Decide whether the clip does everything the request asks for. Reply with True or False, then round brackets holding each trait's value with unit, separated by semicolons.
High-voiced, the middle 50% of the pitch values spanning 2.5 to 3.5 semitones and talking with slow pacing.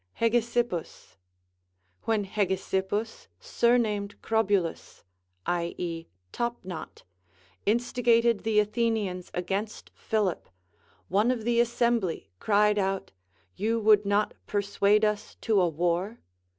True (210 Hz; 3.2 semitones; 100 wpm)